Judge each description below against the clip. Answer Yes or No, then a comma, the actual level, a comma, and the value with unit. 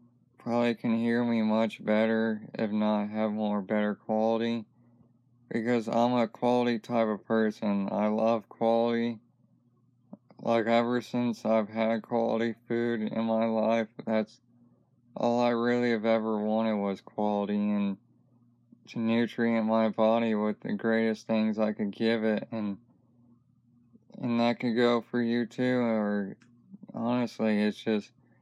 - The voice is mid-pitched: No, low, 115 Hz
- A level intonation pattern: Yes, narrow, 1.5 semitones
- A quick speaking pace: No, average, 140 wpm